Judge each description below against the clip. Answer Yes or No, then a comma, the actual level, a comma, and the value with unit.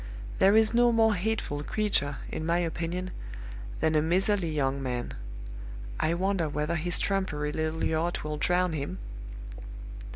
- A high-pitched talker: No, medium, 170 Hz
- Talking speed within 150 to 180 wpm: No, average, 140 wpm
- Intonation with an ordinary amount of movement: Yes, average, 4.2 semitones